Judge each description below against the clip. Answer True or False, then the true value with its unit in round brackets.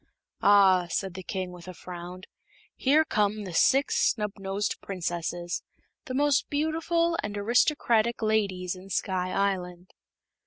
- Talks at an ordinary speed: False (125 wpm)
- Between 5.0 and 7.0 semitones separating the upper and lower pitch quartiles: False (4.5 semitones)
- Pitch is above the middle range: True (195 Hz)